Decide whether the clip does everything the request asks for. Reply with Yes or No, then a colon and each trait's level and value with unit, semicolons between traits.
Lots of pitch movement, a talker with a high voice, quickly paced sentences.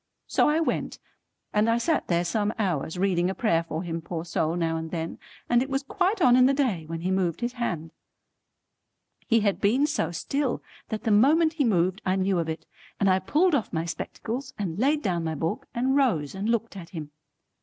Yes: wide, 7.2 semitones; high, 200 Hz; fast, 215 wpm